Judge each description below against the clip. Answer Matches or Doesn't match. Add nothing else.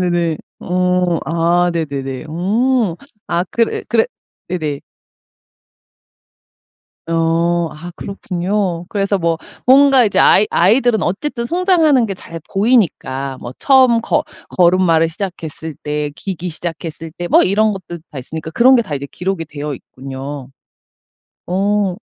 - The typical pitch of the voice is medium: Matches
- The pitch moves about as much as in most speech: Matches